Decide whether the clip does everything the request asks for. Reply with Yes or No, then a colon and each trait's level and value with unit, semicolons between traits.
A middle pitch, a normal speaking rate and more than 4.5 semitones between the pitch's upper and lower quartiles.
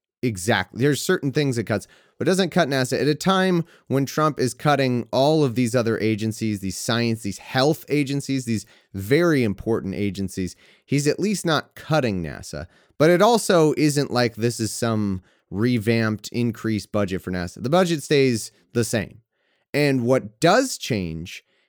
No: low, 120 Hz; average, 165 wpm; average, 5.1 semitones